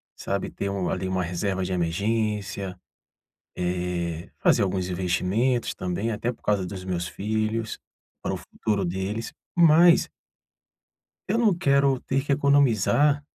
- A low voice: Yes, low, 100 Hz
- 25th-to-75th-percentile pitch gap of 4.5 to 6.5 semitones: Yes, average, 5.0 semitones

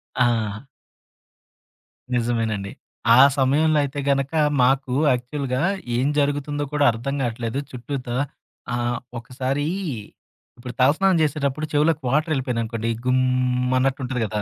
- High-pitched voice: No, low, 130 Hz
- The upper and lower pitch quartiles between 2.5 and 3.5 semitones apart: Yes, average, 2.8 semitones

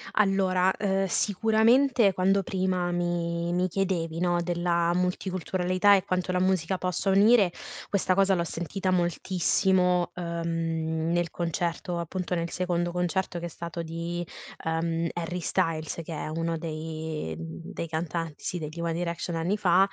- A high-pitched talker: No, medium, 175 Hz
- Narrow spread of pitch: Yes, narrow, 1.9 semitones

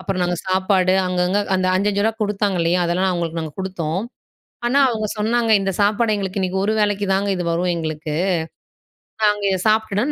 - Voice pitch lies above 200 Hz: No, high, 190 Hz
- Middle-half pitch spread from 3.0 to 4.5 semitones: No, narrow, 2.6 semitones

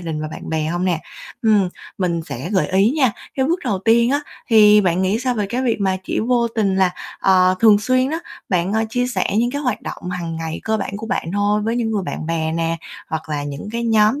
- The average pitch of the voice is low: No, high, 205 Hz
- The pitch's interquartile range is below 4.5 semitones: No, average, 5.0 semitones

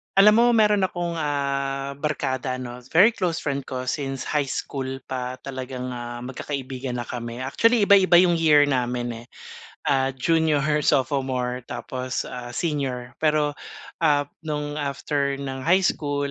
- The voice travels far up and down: No, average, 3.1 semitones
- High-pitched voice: No, medium, 140 Hz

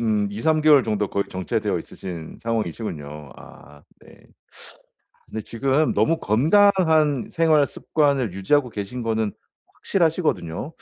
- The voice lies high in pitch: No, low, 115 Hz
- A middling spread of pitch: No, wide, 7.4 semitones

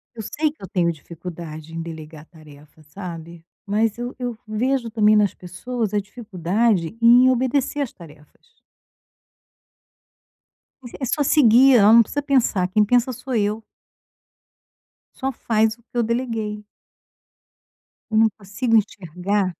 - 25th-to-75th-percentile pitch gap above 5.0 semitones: Yes, wide, 5.4 semitones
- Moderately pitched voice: No, high, 215 Hz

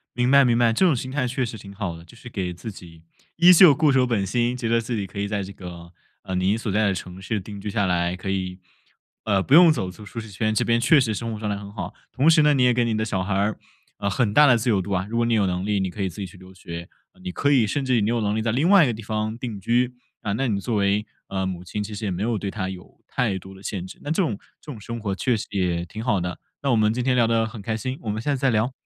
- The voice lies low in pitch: Yes, low, 110 Hz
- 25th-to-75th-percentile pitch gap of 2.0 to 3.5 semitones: No, average, 4.0 semitones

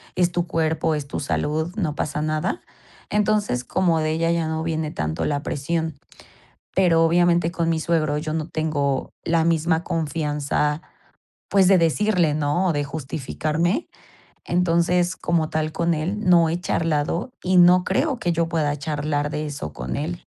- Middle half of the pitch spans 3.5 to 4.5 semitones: No, narrow, 2.5 semitones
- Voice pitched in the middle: Yes, medium, 160 Hz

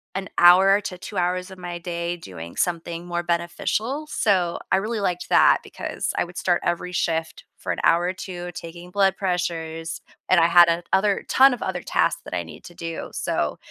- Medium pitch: Yes, medium, 175 Hz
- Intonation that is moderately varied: No, narrow, 1.8 semitones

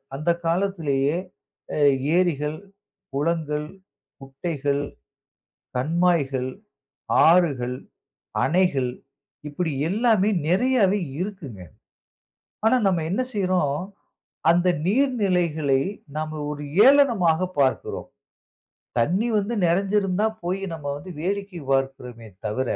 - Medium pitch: Yes, medium, 170 Hz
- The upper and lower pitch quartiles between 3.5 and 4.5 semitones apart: No, average, 5.2 semitones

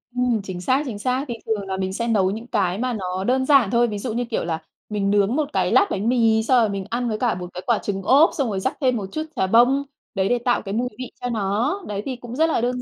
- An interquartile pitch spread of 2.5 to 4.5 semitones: Yes, average, 4.0 semitones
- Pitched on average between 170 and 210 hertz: No, high, 230 Hz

